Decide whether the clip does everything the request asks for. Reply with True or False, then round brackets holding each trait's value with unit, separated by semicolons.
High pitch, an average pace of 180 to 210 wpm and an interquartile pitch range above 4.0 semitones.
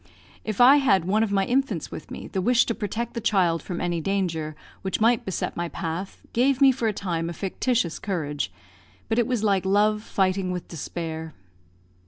True (195 Hz; 195 wpm; 4.9 semitones)